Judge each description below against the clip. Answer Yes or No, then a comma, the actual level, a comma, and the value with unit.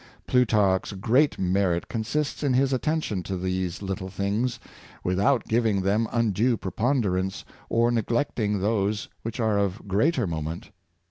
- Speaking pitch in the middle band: No, low, 105 Hz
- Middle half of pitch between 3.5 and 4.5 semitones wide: Yes, average, 3.9 semitones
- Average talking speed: No, slow, 130 wpm